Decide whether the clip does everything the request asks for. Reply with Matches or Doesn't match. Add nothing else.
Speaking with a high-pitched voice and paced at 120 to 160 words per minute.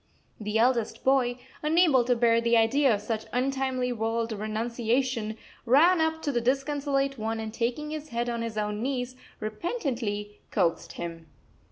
Matches